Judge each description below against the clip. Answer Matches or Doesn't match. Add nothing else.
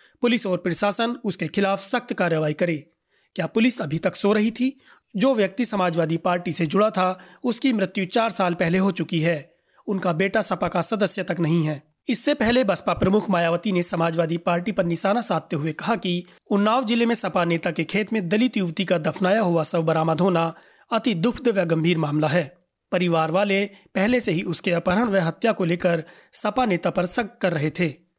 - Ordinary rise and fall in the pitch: Matches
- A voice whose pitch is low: Doesn't match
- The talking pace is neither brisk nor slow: Doesn't match